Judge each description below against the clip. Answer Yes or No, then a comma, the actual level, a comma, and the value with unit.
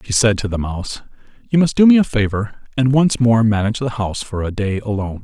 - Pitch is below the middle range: Yes, low, 115 Hz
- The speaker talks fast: Yes, fast, 240 wpm